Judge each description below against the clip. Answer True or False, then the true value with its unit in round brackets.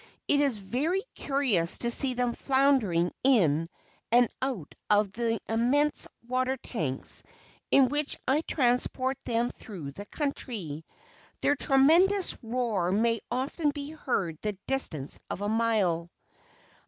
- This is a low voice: False (240 Hz)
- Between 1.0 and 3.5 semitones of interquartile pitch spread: False (5.2 semitones)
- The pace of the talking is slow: True (130 wpm)